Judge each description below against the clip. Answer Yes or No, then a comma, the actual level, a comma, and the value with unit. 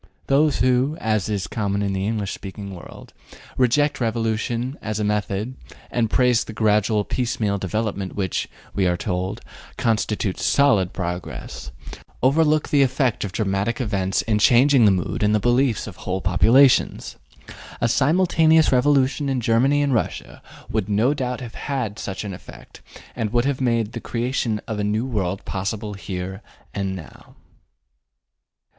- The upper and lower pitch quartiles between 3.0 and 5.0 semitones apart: Yes, average, 4.2 semitones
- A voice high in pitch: No, low, 110 Hz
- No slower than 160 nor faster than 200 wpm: No, average, 150 wpm